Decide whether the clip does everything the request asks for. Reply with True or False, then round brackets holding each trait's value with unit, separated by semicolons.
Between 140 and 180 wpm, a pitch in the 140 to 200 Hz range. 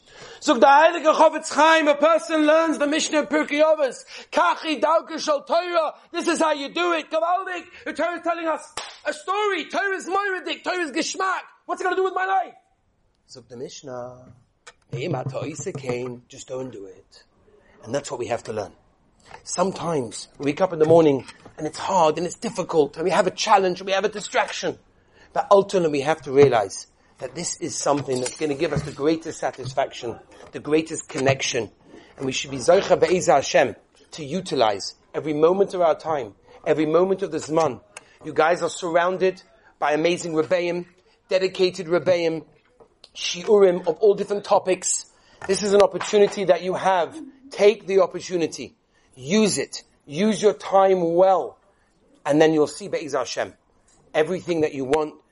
True (175 wpm; 190 Hz)